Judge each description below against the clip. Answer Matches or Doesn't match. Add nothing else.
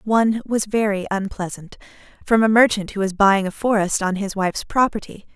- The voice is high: Matches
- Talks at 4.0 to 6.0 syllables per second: Matches